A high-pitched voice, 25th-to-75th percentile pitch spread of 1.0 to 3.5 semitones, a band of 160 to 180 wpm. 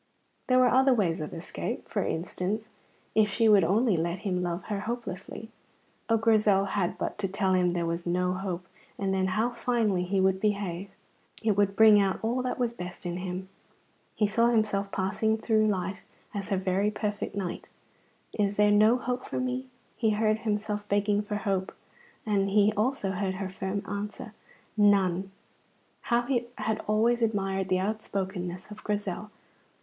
Yes: high, 205 Hz; narrow, 2.5 semitones; average, 170 wpm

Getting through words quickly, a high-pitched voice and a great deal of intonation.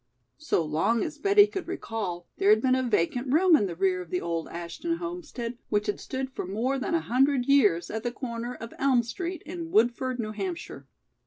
Yes: fast, 210 wpm; high, 245 Hz; wide, 6.8 semitones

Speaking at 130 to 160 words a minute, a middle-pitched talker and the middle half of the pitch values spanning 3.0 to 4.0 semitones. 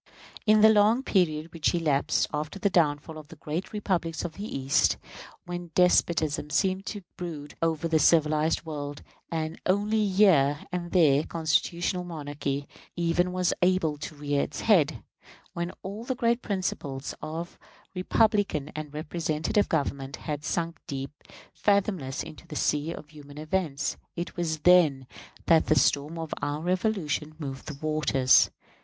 Yes: average, 150 wpm; medium, 160 Hz; average, 3.5 semitones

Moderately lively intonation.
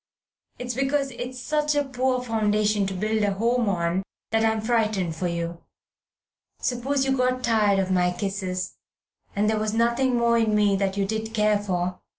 Yes: average, 3.9 semitones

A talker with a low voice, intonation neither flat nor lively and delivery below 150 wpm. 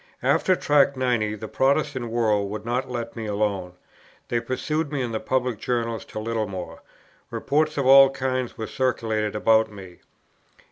No: low, 115 Hz; average, 3.5 semitones; average, 155 wpm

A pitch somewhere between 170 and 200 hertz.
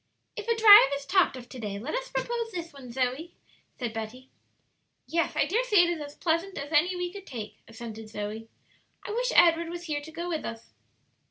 No: very high, 320 Hz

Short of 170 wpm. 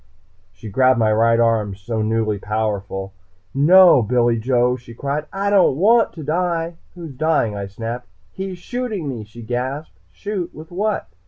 Yes: average, 160 wpm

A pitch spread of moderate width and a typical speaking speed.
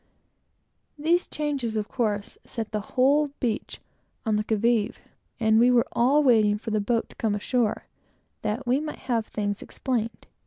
Yes: average, 3.3 semitones; average, 165 wpm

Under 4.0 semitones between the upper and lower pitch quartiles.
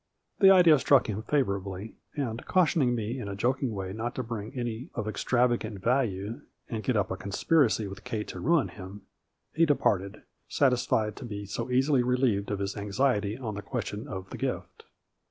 No: average, 4.3 semitones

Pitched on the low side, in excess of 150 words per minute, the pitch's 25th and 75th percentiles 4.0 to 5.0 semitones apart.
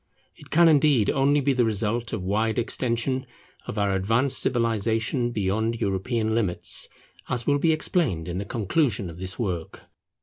Yes: low, 115 Hz; average, 160 wpm; average, 4.6 semitones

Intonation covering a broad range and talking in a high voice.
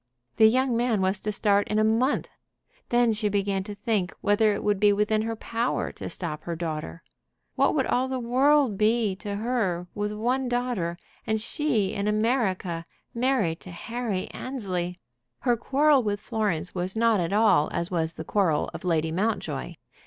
No: average, 4.0 semitones; high, 210 Hz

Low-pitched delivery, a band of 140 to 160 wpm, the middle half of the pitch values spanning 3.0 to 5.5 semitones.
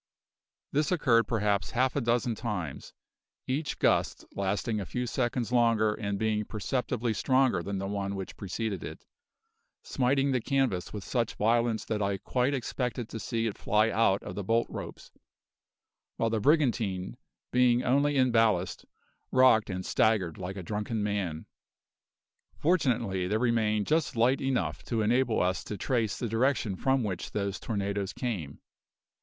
Yes: low, 115 Hz; average, 155 wpm; average, 3.8 semitones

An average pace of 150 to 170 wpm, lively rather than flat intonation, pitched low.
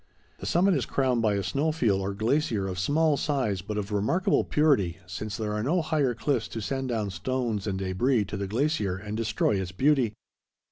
No: average, 200 wpm; wide, 5.8 semitones; low, 110 Hz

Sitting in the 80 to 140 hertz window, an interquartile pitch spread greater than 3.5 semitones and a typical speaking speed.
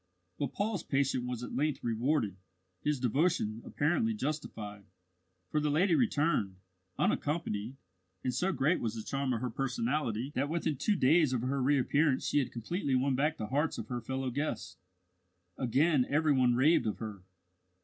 Yes: low, 135 Hz; average, 3.9 semitones; average, 165 wpm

